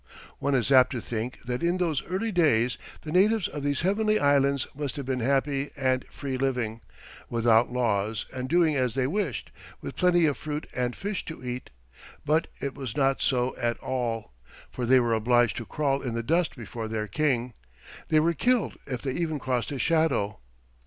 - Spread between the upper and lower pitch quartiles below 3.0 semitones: No, average, 4.2 semitones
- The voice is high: No, low, 135 Hz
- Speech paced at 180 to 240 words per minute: Yes, average, 190 wpm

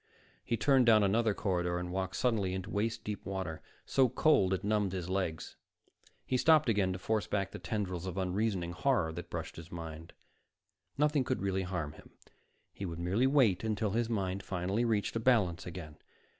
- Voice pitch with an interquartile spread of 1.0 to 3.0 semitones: No, average, 4.0 semitones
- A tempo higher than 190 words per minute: No, average, 185 wpm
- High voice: No, low, 100 Hz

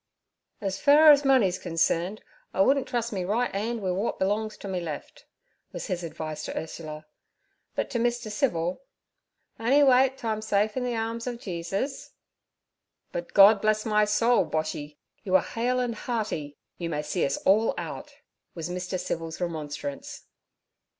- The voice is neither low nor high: No, high, 210 Hz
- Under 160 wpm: No, average, 165 wpm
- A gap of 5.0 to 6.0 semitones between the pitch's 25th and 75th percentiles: Yes, wide, 5.6 semitones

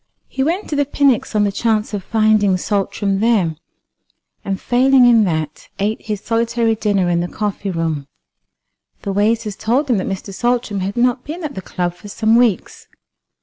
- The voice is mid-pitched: No, high, 215 Hz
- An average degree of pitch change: Yes, average, 3.6 semitones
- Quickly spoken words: No, average, 180 wpm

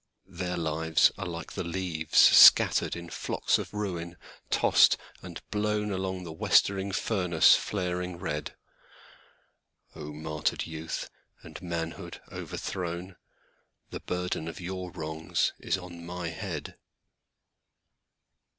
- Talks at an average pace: No, slow, 100 wpm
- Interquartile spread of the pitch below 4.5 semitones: Yes, narrow, 2.4 semitones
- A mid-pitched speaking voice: No, very low, 90 Hz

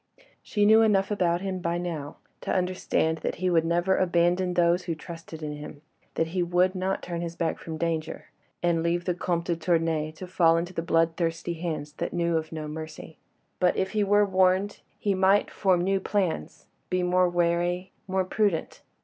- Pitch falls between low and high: Yes, medium, 175 Hz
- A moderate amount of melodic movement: No, narrow, 2.1 semitones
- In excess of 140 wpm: Yes, average, 185 wpm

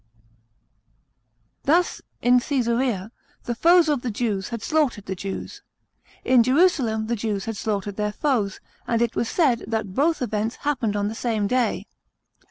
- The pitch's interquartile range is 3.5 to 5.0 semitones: Yes, average, 4.0 semitones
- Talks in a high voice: Yes, high, 235 Hz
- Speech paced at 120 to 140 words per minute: No, average, 155 wpm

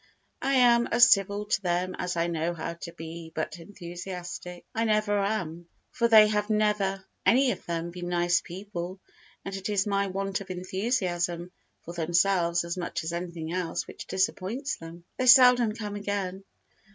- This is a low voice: No, medium, 185 Hz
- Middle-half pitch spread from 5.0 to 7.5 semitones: No, average, 3.3 semitones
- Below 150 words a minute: No, average, 170 wpm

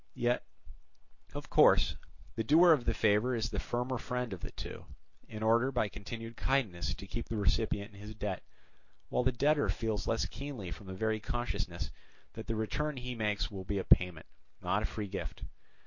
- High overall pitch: No, low, 110 Hz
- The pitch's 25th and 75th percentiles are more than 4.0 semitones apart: No, average, 3.3 semitones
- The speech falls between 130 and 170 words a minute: No, average, 190 wpm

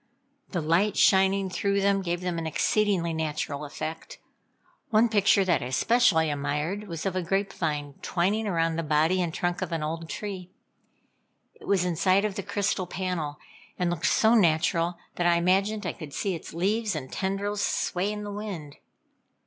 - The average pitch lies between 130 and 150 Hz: No, medium, 180 Hz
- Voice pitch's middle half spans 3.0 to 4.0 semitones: Yes, average, 3.5 semitones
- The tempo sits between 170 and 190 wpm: Yes, average, 175 wpm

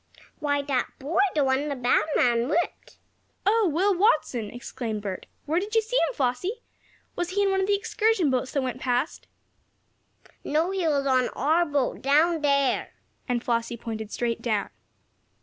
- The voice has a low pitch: No, very high, 285 Hz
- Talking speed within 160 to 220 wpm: Yes, average, 170 wpm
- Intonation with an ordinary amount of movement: No, wide, 6.1 semitones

